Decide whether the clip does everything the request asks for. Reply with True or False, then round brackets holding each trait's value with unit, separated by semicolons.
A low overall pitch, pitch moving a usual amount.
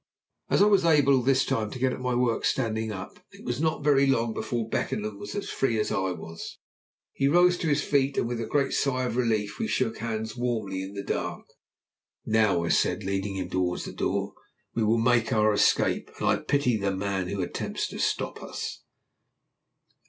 True (115 Hz; 4.6 semitones)